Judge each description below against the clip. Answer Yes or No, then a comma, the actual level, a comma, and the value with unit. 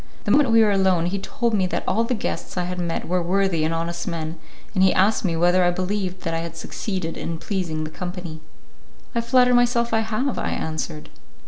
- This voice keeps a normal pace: No, fast, 220 wpm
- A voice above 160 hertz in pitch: Yes, medium, 185 Hz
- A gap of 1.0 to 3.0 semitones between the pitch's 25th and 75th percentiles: No, average, 4.3 semitones